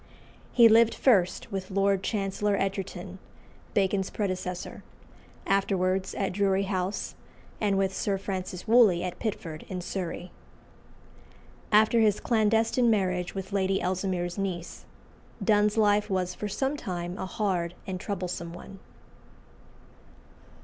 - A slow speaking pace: Yes, slow, 120 wpm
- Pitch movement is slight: Yes, narrow, 2.1 semitones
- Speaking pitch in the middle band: No, high, 195 Hz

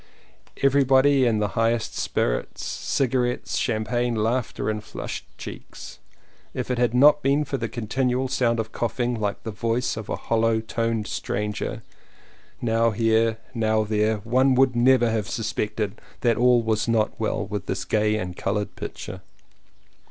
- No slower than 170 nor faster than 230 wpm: No, average, 150 wpm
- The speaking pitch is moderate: No, low, 115 Hz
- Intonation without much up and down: Yes, narrow, 2.3 semitones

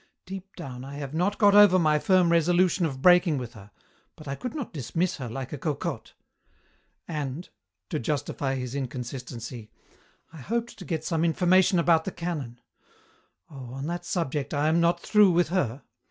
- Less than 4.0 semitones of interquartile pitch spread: No, average, 4.9 semitones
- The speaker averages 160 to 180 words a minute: Yes, average, 175 wpm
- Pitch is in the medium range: Yes, medium, 160 Hz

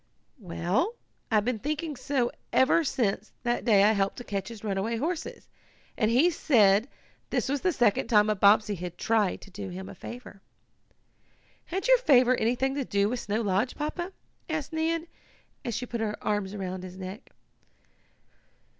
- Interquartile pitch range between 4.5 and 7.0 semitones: Yes, average, 5.1 semitones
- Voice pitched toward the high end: Yes, high, 225 Hz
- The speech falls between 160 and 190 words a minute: Yes, average, 170 wpm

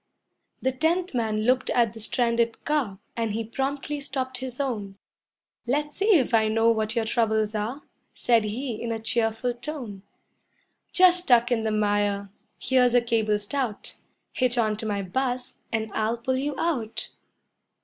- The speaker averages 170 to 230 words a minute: No, average, 160 wpm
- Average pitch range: Yes, average, 3.1 semitones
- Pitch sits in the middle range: No, high, 235 Hz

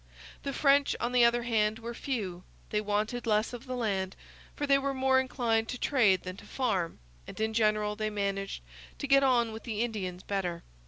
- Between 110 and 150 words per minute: No, average, 200 wpm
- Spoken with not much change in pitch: No, average, 3.4 semitones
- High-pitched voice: Yes, high, 225 Hz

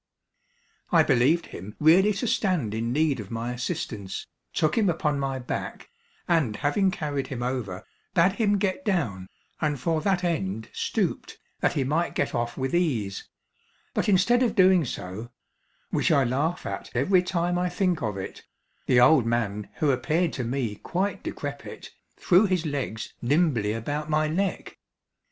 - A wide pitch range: Yes, wide, 7.0 semitones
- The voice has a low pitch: No, medium, 150 Hz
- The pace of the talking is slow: No, average, 160 wpm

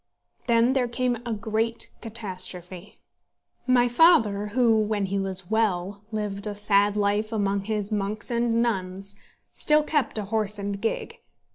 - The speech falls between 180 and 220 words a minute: No, average, 145 wpm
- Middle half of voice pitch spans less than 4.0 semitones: Yes, narrow, 2.6 semitones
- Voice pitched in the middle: No, high, 210 Hz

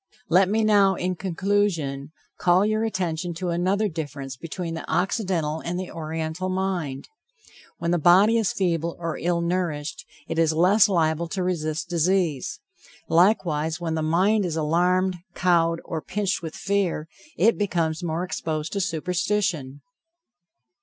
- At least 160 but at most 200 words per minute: No, average, 145 wpm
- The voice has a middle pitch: Yes, medium, 175 Hz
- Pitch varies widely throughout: No, average, 2.9 semitones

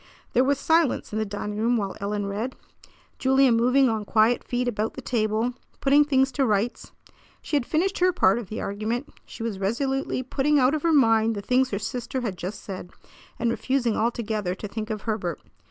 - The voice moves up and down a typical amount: Yes, average, 3.9 semitones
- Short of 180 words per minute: No, average, 200 wpm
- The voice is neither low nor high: No, high, 235 Hz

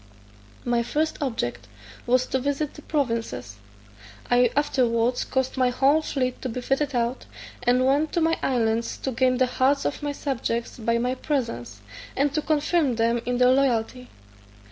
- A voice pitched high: Yes, very high, 255 Hz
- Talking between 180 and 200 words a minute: No, average, 165 wpm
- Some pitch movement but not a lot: Yes, average, 3.1 semitones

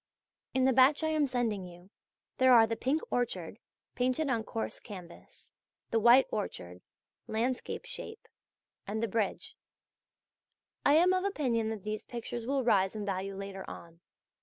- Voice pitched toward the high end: Yes, high, 230 Hz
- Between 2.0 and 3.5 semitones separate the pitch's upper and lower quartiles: No, average, 4.8 semitones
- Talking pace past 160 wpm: No, average, 155 wpm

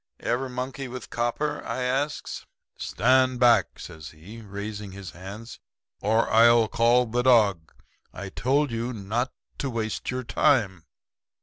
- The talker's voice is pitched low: Yes, low, 115 Hz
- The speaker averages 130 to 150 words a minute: Yes, slow, 135 wpm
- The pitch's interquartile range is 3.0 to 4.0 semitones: Yes, average, 3.6 semitones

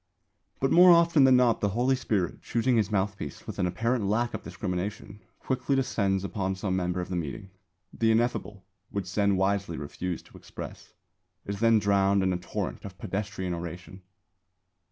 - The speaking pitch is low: Yes, low, 100 Hz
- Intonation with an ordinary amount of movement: Yes, average, 3.6 semitones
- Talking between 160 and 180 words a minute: Yes, average, 170 wpm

